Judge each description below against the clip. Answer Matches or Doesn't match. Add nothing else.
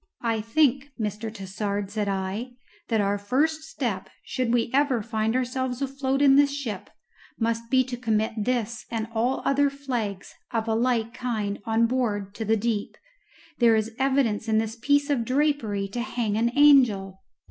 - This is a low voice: Doesn't match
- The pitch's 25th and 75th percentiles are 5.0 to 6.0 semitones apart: Doesn't match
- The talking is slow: Doesn't match